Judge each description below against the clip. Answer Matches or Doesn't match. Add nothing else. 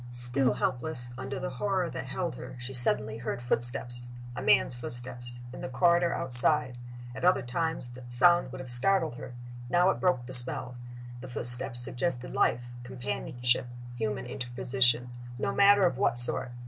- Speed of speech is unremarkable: Matches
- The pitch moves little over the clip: Matches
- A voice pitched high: Doesn't match